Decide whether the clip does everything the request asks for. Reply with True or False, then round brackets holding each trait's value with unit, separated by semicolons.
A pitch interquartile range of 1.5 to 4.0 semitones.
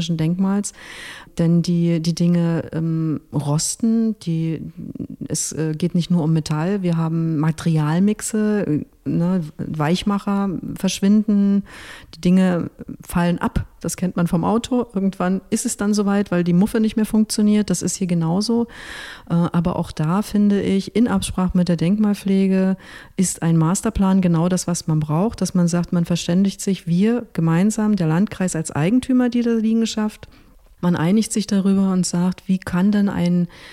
True (3.3 semitones)